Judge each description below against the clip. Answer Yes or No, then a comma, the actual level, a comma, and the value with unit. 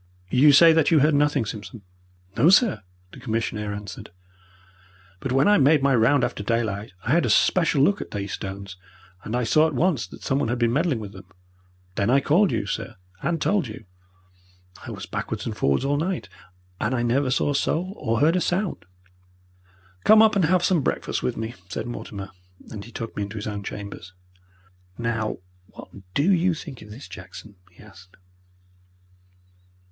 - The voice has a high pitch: No, low, 125 Hz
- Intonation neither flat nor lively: No, wide, 6.9 semitones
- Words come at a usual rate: Yes, average, 185 wpm